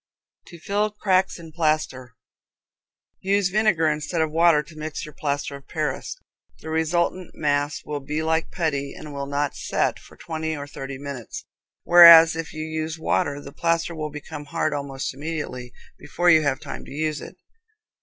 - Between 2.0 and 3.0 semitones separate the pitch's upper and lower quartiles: Yes, narrow, 2.6 semitones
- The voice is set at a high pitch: No, medium, 155 Hz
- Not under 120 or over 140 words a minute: No, average, 170 wpm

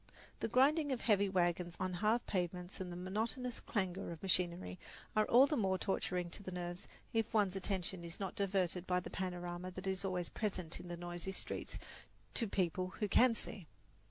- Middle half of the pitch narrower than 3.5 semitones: Yes, average, 2.8 semitones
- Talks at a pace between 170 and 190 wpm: Yes, average, 185 wpm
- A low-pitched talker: No, medium, 185 Hz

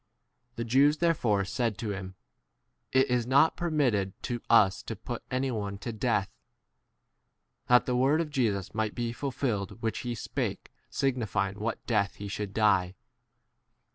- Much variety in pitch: No, average, 4.1 semitones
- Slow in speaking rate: No, average, 165 wpm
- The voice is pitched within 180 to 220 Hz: No, low, 115 Hz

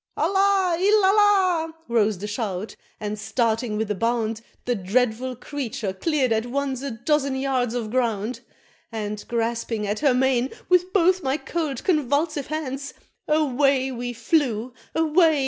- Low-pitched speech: No, very high, 255 Hz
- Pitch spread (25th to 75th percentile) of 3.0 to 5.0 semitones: No, wide, 5.4 semitones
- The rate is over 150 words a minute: No, average, 145 wpm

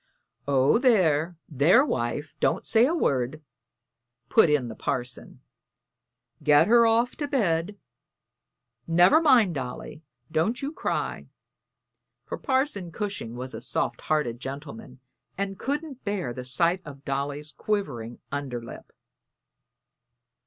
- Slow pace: Yes, slow, 120 wpm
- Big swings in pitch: Yes, wide, 8.5 semitones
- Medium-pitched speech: Yes, medium, 160 Hz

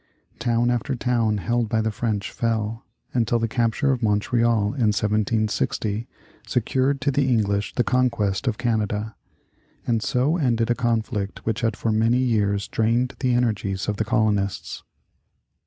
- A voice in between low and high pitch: No, low, 115 Hz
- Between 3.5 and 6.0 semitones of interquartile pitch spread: No, narrow, 2.4 semitones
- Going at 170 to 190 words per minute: No, average, 150 wpm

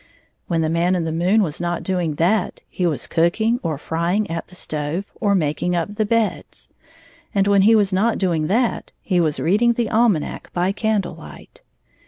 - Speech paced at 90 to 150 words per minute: No, average, 190 wpm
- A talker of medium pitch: Yes, medium, 180 Hz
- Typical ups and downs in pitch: Yes, average, 4.1 semitones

